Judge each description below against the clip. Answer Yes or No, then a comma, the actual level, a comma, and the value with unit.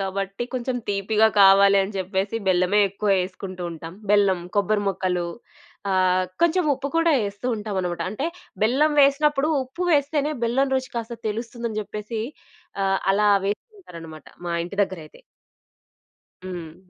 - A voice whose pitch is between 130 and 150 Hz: No, high, 205 Hz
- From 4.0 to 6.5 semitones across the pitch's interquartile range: Yes, average, 5.0 semitones